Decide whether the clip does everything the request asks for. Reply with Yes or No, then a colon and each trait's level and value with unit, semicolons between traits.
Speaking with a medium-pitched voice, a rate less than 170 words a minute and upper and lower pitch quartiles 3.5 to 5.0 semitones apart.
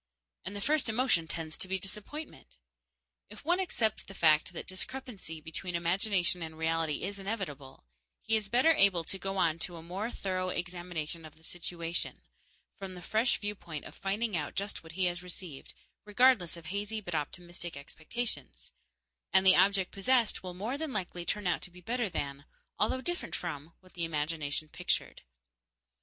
No: medium, 180 Hz; average, 175 wpm; average, 4.0 semitones